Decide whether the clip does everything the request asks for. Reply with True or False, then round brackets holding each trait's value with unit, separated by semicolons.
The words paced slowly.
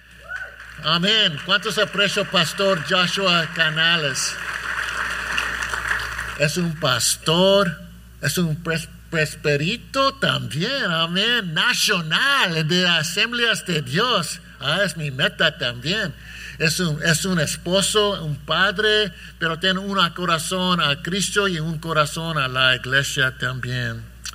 True (110 wpm)